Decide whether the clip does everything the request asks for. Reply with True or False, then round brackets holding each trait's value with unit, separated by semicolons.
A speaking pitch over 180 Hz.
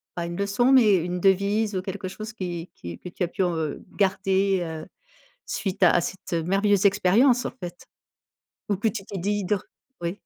True (190 Hz)